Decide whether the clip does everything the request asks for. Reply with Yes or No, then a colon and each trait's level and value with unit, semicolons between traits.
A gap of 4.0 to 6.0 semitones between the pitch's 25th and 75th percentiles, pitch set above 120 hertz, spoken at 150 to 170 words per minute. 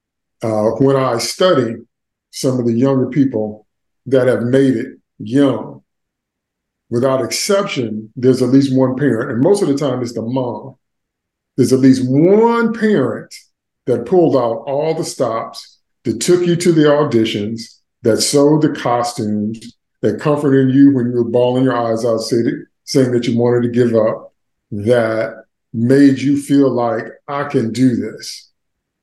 No: average, 3.3 semitones; low, 130 Hz; average, 160 wpm